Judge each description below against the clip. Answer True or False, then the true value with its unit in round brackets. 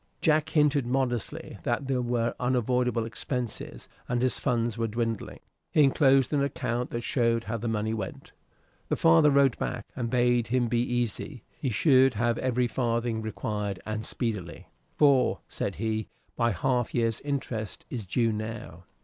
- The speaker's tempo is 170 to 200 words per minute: False (160 wpm)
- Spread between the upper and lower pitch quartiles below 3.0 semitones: True (2.4 semitones)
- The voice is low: True (120 Hz)